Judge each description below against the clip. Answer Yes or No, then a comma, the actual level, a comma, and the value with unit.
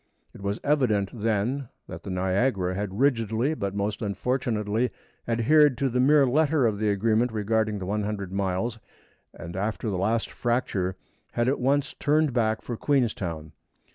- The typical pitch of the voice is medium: No, low, 110 Hz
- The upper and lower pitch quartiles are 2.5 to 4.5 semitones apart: Yes, average, 4.1 semitones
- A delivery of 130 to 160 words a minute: Yes, average, 155 wpm